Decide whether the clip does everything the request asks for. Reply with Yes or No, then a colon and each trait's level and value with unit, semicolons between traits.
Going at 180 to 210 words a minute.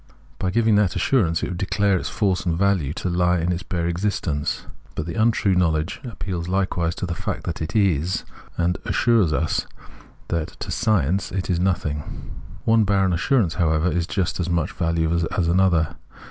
Yes: average, 190 wpm